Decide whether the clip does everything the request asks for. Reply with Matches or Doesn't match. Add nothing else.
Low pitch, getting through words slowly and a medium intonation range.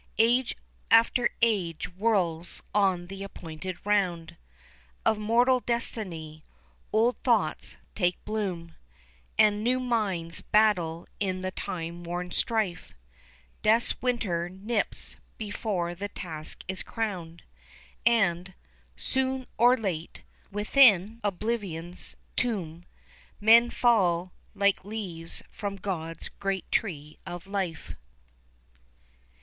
Doesn't match